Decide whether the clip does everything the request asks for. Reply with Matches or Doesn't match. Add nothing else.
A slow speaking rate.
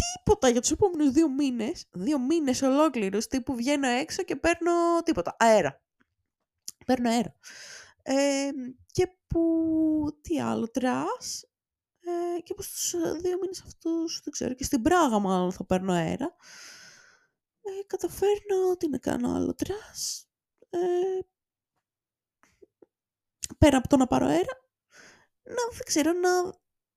Doesn't match